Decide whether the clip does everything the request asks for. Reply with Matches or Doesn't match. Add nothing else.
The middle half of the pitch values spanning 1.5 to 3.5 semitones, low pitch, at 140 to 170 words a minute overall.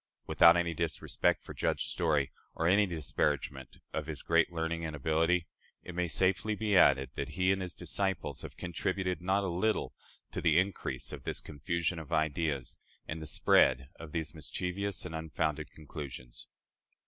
Matches